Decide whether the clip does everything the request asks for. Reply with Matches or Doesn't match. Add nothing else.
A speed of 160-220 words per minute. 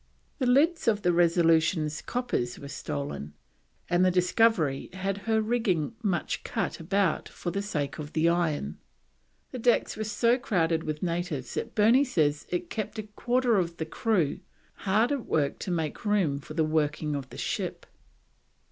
Matches